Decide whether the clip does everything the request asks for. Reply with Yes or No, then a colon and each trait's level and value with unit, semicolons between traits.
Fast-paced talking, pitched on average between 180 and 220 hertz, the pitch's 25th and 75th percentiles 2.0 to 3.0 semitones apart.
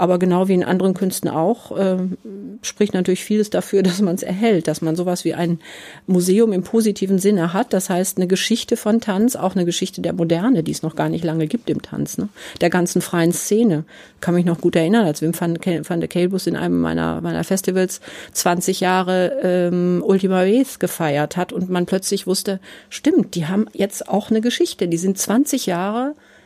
Yes: fast, 200 wpm; medium, 185 Hz; narrow, 2.6 semitones